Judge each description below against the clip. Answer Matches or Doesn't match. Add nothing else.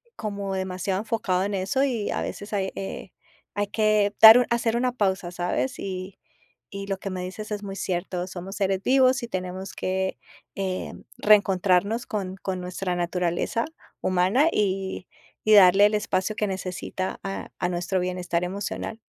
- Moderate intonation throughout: Doesn't match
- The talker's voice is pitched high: Matches